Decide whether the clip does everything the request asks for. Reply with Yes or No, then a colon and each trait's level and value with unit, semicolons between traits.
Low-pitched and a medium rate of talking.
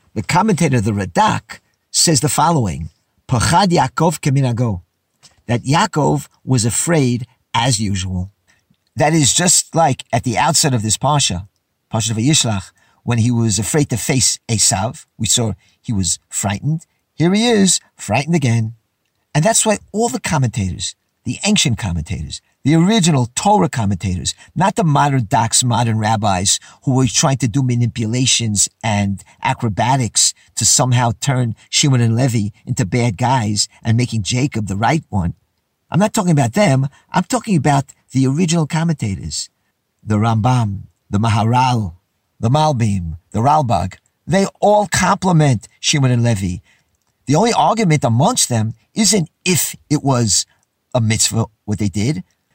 Yes: low, 120 Hz; average, 145 wpm